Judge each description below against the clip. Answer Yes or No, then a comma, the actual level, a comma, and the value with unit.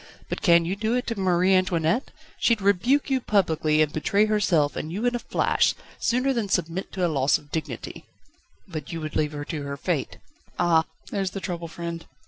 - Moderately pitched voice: Yes, medium, 180 Hz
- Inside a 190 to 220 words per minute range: Yes, average, 200 wpm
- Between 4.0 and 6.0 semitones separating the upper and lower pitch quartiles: Yes, average, 4.6 semitones